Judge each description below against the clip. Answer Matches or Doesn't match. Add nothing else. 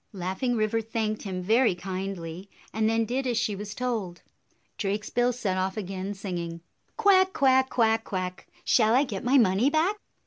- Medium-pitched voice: Doesn't match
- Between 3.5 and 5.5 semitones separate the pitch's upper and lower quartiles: Matches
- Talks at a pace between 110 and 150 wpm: Doesn't match